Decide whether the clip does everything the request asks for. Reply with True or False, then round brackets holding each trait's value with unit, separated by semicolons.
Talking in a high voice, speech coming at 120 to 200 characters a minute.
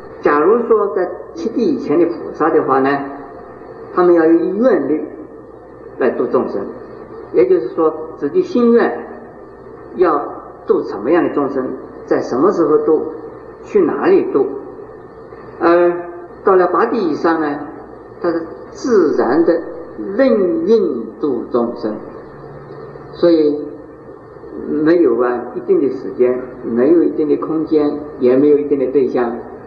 True (365 Hz; 190 characters per minute)